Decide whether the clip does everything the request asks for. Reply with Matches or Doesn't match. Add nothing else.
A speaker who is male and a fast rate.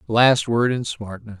Doesn't match